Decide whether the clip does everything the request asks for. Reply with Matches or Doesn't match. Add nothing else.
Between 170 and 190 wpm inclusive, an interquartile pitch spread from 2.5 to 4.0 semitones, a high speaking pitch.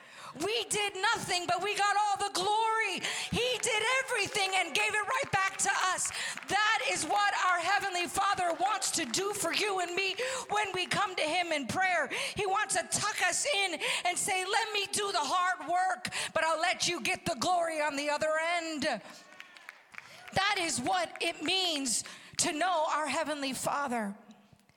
Matches